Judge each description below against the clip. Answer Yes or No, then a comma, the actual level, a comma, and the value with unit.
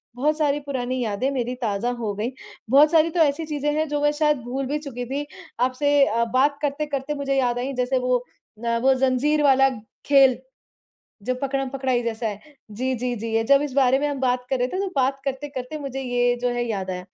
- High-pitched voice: Yes, very high, 265 Hz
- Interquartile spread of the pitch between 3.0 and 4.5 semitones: No, narrow, 2.6 semitones